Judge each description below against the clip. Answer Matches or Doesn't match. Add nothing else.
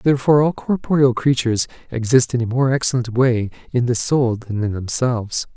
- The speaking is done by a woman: Doesn't match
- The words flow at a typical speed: Matches